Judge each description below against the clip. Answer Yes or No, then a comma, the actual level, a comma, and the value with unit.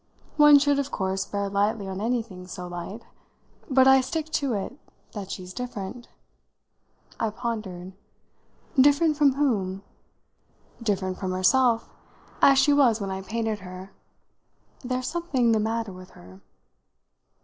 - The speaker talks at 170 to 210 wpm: No, slow, 135 wpm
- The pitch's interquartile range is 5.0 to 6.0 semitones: Yes, wide, 5.6 semitones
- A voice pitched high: Yes, high, 220 Hz